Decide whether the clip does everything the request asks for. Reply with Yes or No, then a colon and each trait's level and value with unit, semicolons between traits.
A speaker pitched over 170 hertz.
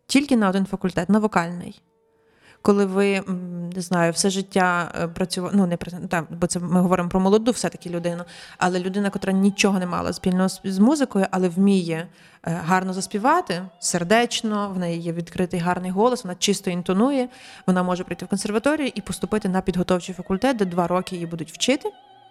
Yes: medium, 185 Hz